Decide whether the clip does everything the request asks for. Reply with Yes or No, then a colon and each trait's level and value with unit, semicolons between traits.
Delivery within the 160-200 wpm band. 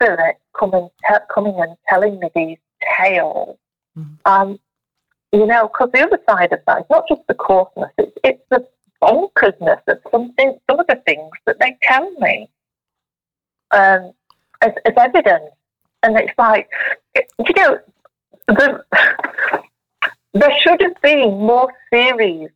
No: average, 140 wpm